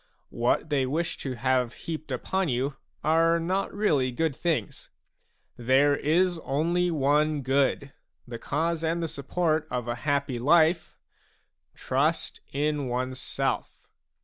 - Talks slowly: Yes, slow, 130 wpm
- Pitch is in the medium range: Yes, medium, 145 Hz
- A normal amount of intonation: Yes, average, 4.0 semitones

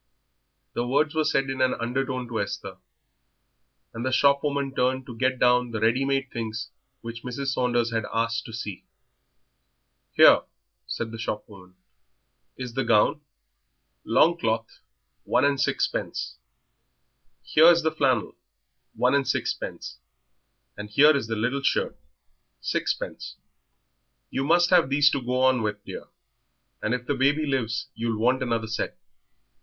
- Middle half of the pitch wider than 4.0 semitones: No, average, 3.3 semitones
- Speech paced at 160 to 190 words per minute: No, average, 145 wpm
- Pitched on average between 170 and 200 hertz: No, low, 125 Hz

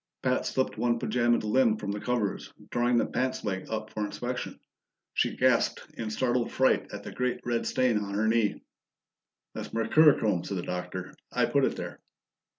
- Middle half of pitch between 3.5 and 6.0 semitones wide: No, average, 3.0 semitones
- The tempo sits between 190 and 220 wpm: No, average, 175 wpm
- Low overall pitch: Yes, low, 115 Hz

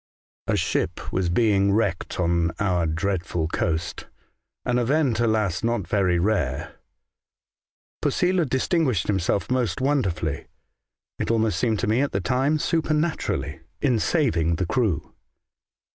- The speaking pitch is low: Yes, low, 105 Hz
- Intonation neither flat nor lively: No, wide, 6.5 semitones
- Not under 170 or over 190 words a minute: No, average, 145 wpm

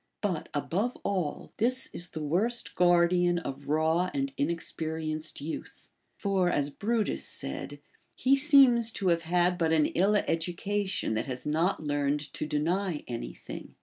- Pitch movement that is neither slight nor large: Yes, average, 4.7 semitones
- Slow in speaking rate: No, average, 150 wpm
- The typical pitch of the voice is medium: Yes, medium, 170 Hz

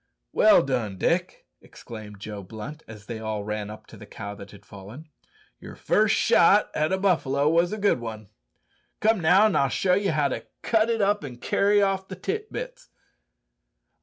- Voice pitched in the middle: Yes, medium, 145 Hz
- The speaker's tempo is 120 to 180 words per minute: No, average, 190 wpm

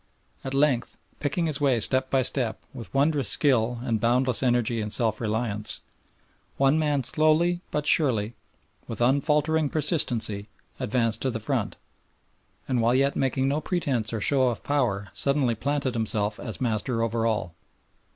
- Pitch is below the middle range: Yes, low, 125 Hz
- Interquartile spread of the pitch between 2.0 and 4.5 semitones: Yes, average, 4.0 semitones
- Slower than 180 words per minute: Yes, average, 150 wpm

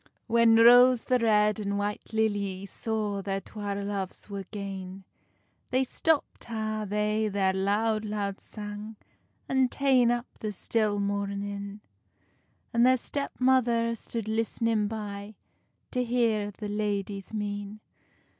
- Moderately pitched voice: No, high, 210 Hz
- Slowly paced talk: Yes, slow, 125 wpm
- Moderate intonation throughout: No, narrow, 2.3 semitones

